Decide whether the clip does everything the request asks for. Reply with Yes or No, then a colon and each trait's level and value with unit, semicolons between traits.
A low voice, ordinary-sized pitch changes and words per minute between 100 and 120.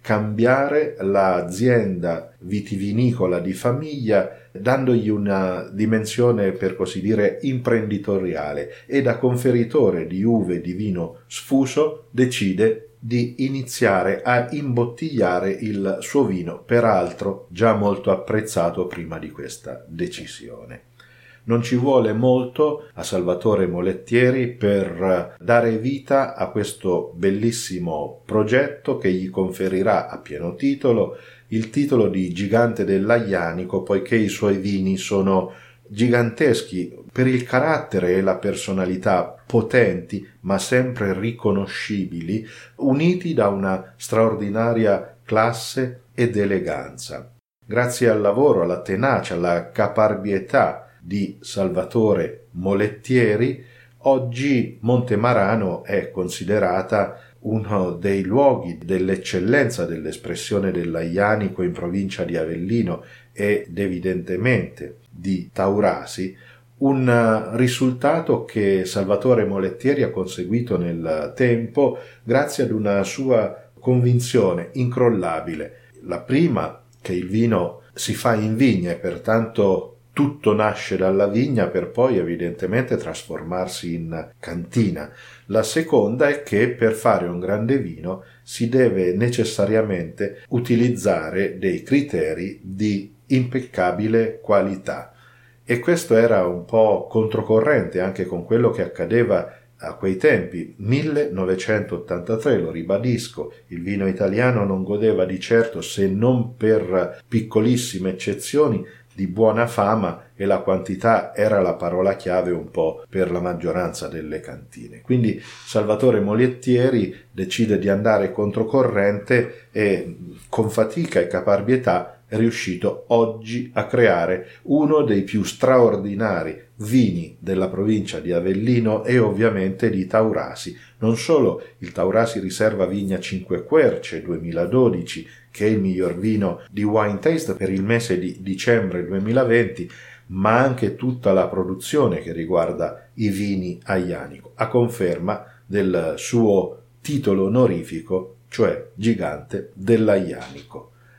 Yes: low, 110 Hz; average, 4.3 semitones; slow, 115 wpm